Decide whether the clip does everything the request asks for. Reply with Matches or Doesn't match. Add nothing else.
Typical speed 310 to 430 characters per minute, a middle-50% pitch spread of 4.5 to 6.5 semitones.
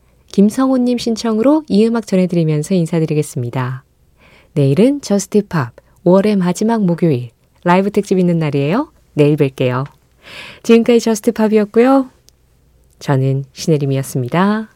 Doesn't match